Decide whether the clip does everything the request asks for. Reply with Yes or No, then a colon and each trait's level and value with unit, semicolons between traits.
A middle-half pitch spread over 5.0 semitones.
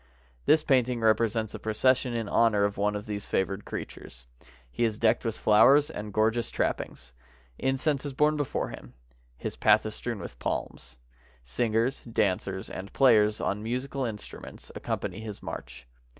No: average, 3.5 semitones